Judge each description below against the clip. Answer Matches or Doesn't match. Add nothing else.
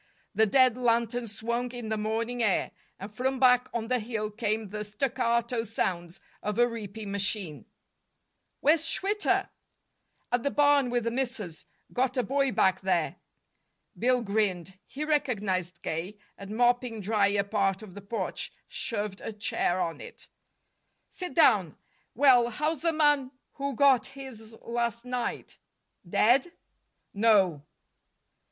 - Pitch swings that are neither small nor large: Matches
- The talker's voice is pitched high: Matches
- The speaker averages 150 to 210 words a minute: Doesn't match